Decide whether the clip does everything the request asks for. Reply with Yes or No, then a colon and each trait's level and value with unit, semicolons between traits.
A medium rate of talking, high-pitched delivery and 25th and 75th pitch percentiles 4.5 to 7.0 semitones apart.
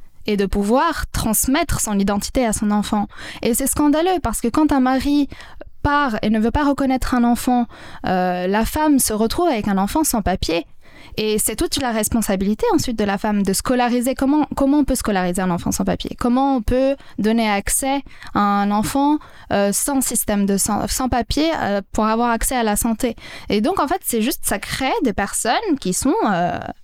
Yes: average, 200 wpm; high, 235 Hz; average, 4.8 semitones